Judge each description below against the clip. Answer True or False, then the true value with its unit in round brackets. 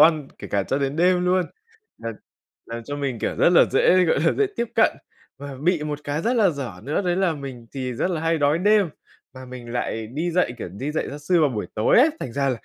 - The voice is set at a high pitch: False (145 Hz)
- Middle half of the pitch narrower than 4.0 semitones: False (5.6 semitones)